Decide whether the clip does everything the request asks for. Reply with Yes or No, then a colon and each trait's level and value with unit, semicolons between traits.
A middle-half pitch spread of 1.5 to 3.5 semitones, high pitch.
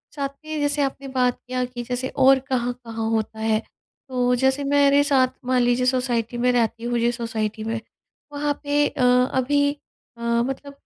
Yes: narrow, 2.5 semitones; very high, 250 Hz